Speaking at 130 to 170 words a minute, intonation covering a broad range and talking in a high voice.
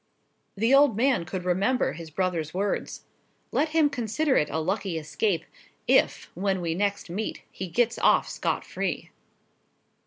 Yes: average, 150 wpm; wide, 5.7 semitones; high, 195 Hz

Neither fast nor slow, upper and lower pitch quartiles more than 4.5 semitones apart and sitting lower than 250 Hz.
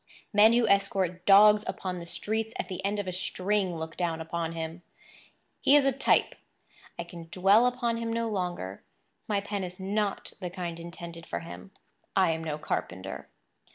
No: average, 180 wpm; average, 3.6 semitones; medium, 185 Hz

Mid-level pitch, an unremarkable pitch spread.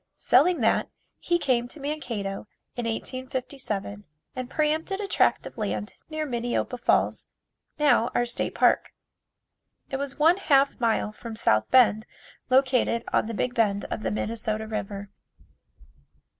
No: high, 245 Hz; average, 4.2 semitones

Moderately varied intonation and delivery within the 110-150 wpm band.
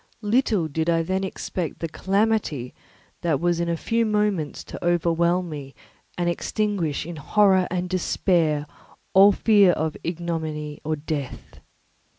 Yes: average, 3.4 semitones; average, 140 wpm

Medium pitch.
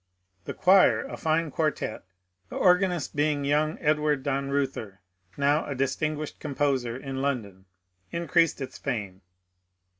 Yes: medium, 145 Hz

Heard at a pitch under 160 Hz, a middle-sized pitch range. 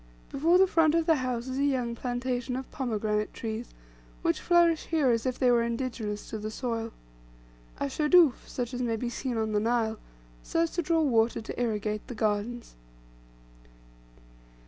No: high, 245 Hz; average, 3.8 semitones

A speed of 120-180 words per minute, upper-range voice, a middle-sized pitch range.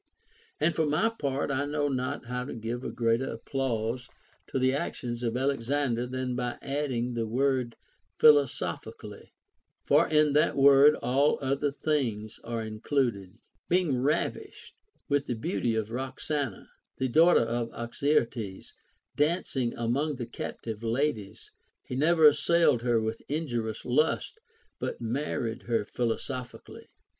No: average, 140 wpm; low, 130 Hz; average, 3.7 semitones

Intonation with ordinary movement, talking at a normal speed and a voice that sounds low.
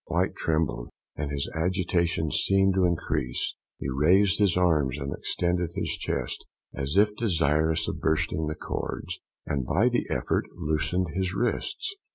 Yes: average, 3.7 semitones; average, 150 wpm; very low, 80 Hz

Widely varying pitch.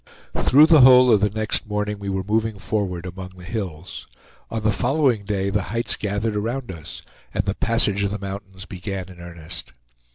No: average, 3.0 semitones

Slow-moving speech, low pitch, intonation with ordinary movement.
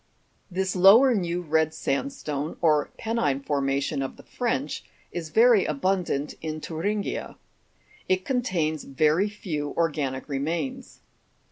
No: slow, 120 wpm; medium, 160 Hz; average, 4.7 semitones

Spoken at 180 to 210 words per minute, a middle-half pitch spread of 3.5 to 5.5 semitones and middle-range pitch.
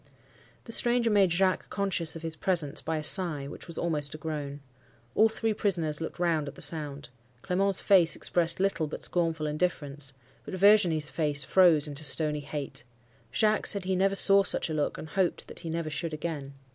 Yes: average, 190 wpm; average, 3.9 semitones; medium, 165 Hz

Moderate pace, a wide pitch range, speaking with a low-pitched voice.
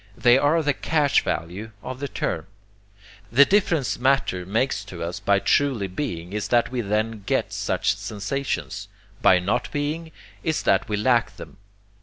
Yes: average, 160 wpm; wide, 6.1 semitones; low, 115 Hz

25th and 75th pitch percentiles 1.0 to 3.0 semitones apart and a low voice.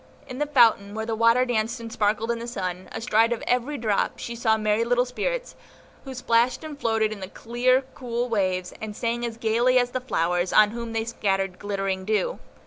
No: average, 2.7 semitones; high, 230 Hz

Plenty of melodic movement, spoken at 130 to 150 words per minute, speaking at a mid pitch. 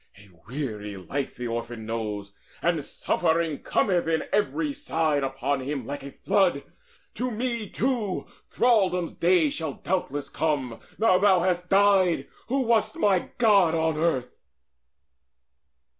Yes: wide, 6.7 semitones; slow, 135 wpm; medium, 165 Hz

